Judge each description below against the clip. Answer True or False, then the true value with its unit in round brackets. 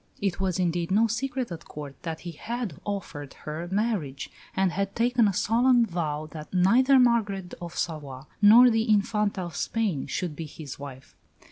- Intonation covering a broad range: True (5.9 semitones)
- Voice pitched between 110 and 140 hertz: False (190 Hz)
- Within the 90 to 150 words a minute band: False (170 wpm)